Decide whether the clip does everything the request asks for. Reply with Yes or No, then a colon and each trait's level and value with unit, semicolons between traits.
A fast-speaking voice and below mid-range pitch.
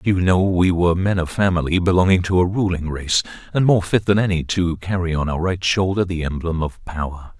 Yes: fast, 220 wpm; very low, 90 Hz